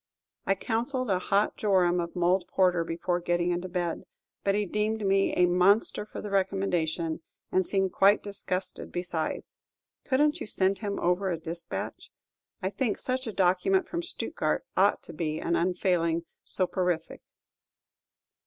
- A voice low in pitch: No, medium, 185 Hz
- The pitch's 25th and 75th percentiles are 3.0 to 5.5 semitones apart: No, narrow, 2.6 semitones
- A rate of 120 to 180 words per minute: Yes, average, 155 wpm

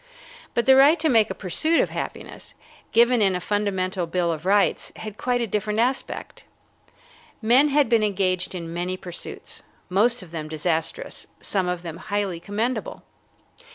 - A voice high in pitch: Yes, high, 200 Hz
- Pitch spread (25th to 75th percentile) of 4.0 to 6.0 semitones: Yes, average, 4.7 semitones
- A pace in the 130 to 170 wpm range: Yes, average, 160 wpm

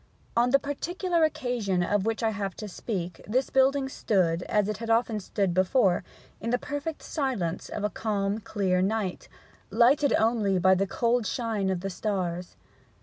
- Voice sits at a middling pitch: No, high, 215 Hz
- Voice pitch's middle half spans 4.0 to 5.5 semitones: Yes, average, 4.5 semitones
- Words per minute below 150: No, average, 170 wpm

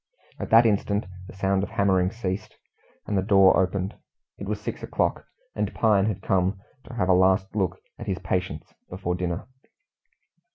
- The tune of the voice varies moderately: No, narrow, 1.9 semitones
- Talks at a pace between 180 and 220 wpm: No, average, 170 wpm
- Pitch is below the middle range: Yes, very low, 95 Hz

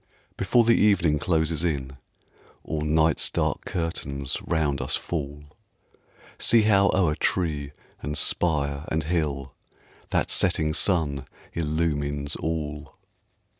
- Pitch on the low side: Yes, very low, 75 Hz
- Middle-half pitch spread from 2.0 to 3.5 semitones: Yes, average, 2.7 semitones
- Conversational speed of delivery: No, slow, 110 wpm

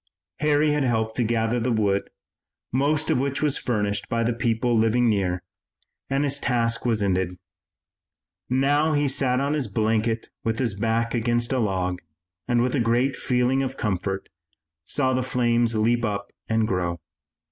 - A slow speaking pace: No, average, 165 wpm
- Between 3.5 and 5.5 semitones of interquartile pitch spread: No, average, 3.1 semitones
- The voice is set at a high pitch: No, low, 120 Hz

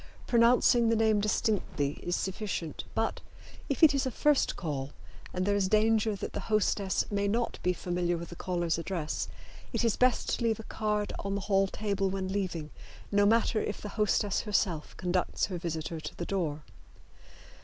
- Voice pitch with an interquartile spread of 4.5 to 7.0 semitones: No, average, 3.6 semitones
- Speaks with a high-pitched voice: Yes, high, 200 Hz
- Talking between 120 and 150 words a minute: No, average, 180 wpm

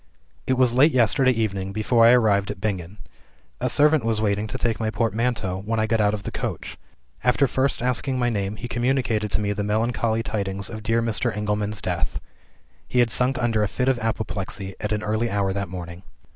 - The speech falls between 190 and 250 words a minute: Yes, fast, 205 wpm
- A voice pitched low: Yes, low, 110 Hz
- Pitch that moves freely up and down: No, average, 2.8 semitones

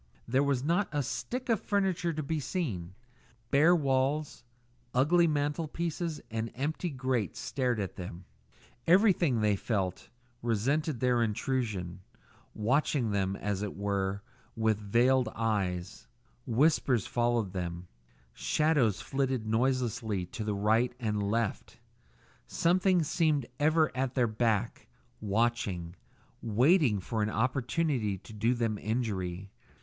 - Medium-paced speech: No, slow, 120 wpm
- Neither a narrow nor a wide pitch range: No, wide, 5.8 semitones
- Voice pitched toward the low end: Yes, low, 120 Hz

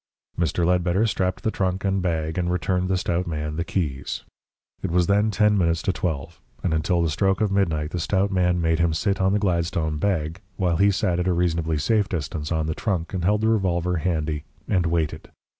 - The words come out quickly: Yes, fast, 210 wpm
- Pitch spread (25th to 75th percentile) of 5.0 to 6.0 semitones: No, average, 2.9 semitones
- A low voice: Yes, very low, 90 Hz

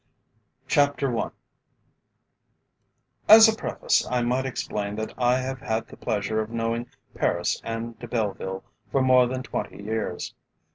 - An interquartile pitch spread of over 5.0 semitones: No, average, 2.8 semitones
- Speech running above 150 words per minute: No, average, 140 wpm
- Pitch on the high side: No, low, 120 Hz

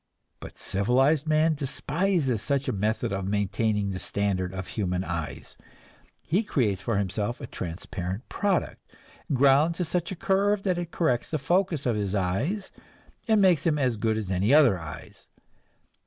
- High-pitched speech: No, low, 125 Hz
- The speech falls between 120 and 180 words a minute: Yes, average, 160 wpm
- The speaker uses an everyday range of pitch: No, wide, 8.4 semitones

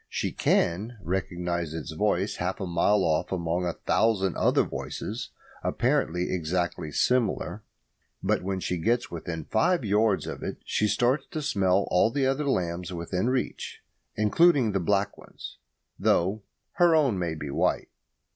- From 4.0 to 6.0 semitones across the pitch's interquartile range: Yes, average, 4.6 semitones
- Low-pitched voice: Yes, very low, 95 Hz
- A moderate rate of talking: Yes, average, 150 wpm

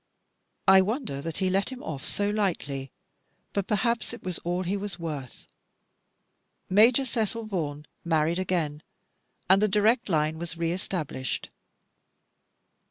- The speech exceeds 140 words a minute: No, slow, 135 wpm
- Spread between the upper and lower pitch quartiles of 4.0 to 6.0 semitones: Yes, average, 4.7 semitones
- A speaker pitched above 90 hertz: Yes, medium, 185 Hz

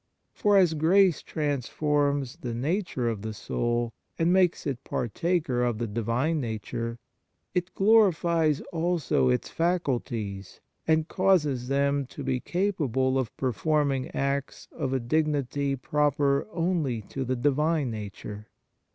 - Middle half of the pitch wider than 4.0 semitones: Yes, average, 5.1 semitones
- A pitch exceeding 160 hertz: No, medium, 140 Hz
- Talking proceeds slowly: Yes, slow, 125 wpm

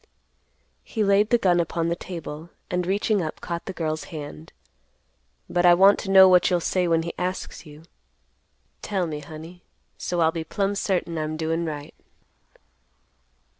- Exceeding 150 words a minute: Yes, average, 165 wpm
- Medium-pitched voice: Yes, medium, 170 Hz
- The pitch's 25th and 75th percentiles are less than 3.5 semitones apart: Yes, average, 2.8 semitones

